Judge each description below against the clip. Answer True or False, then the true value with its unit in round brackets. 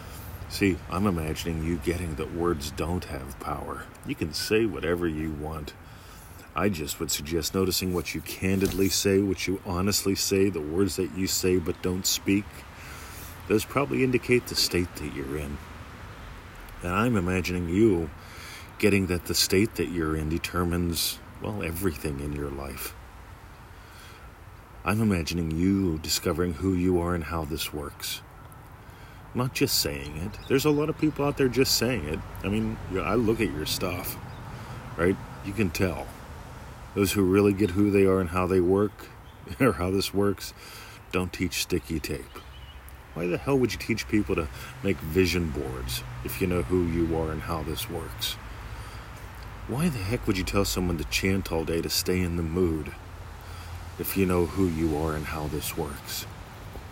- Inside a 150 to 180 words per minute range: True (175 wpm)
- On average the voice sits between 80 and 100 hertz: True (90 Hz)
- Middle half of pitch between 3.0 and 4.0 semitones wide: True (3.6 semitones)